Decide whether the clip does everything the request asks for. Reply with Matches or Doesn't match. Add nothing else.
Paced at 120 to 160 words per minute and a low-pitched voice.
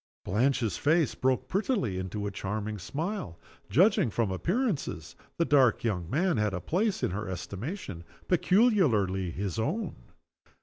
Matches